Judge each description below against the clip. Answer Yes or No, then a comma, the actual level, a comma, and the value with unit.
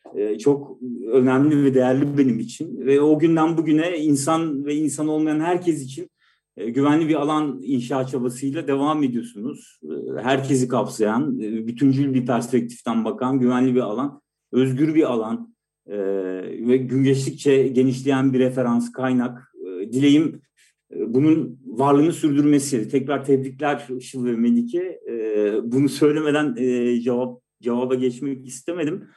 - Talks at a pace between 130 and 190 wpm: No, average, 115 wpm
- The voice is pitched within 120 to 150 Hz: Yes, low, 135 Hz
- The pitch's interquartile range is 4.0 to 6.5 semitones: No, average, 3.2 semitones